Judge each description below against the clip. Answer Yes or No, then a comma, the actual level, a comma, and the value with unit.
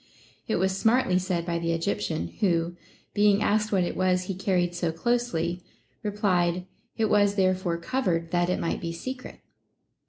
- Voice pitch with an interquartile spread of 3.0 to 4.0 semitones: Yes, average, 3.3 semitones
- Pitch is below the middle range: No, medium, 185 Hz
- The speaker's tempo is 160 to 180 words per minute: Yes, average, 165 wpm